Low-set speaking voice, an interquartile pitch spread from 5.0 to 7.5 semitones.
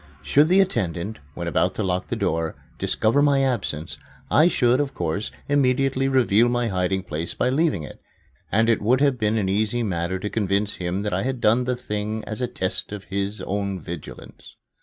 Yes: low, 105 Hz; average, 5.3 semitones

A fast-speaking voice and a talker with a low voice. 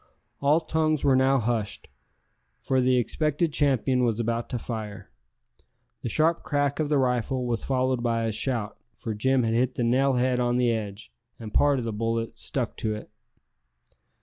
No: average, 175 wpm; low, 125 Hz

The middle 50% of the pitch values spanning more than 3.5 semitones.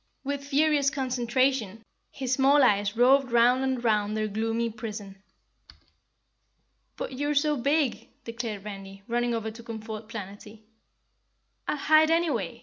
Yes: average, 4.1 semitones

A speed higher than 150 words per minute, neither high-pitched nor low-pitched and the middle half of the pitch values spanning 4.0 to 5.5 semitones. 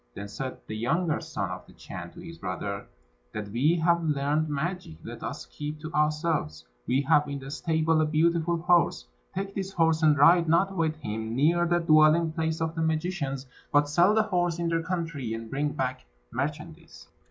No: average, 190 wpm; medium, 155 Hz; average, 3.1 semitones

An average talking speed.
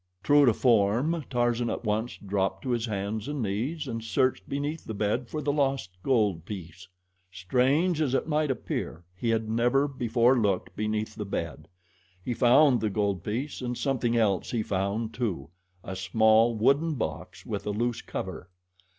Yes: average, 170 wpm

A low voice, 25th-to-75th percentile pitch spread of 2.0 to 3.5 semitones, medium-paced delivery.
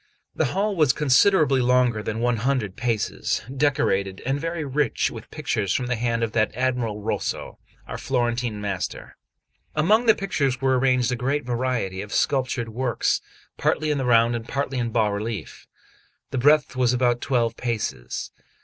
Yes: low, 125 Hz; average, 3.2 semitones; average, 160 wpm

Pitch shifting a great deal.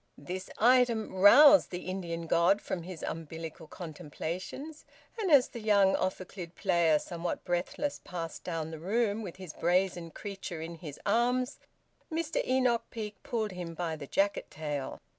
No: average, 5.0 semitones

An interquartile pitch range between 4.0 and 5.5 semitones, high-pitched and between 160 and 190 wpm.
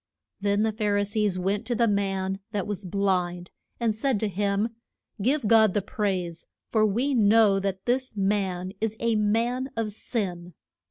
No: narrow, 2.5 semitones; high, 205 Hz; average, 170 wpm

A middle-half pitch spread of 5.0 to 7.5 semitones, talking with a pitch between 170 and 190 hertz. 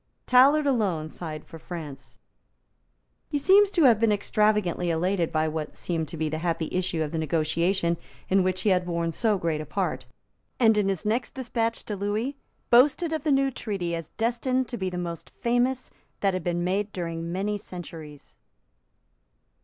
Yes: wide, 5.6 semitones; medium, 185 Hz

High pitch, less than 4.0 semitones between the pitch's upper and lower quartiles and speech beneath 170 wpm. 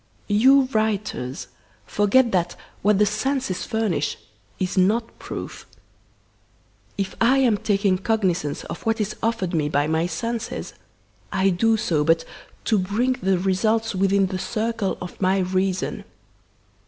Yes: high, 195 Hz; average, 3.5 semitones; slow, 135 wpm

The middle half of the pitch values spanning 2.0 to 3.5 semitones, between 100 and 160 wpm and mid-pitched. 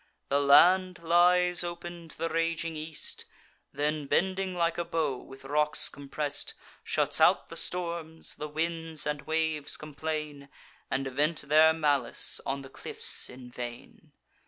Yes: average, 2.8 semitones; average, 140 wpm; medium, 155 Hz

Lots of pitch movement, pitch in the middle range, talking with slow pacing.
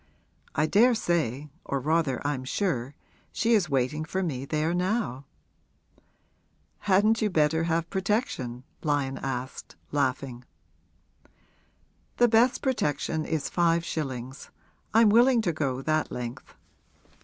Yes: wide, 6.5 semitones; medium, 155 Hz; slow, 115 wpm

